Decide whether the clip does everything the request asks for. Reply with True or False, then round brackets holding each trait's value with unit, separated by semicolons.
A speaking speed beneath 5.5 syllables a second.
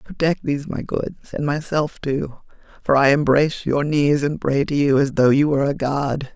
True (5.2 syllables/s)